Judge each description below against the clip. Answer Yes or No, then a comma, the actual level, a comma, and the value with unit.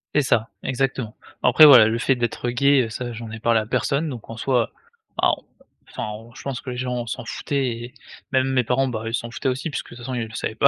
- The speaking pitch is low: Yes, low, 125 Hz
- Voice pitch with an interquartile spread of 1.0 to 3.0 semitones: Yes, narrow, 2.5 semitones